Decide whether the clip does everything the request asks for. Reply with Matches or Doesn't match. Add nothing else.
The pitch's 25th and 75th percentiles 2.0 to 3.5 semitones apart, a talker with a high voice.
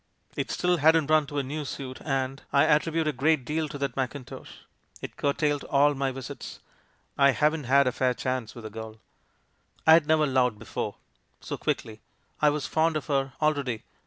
Doesn't match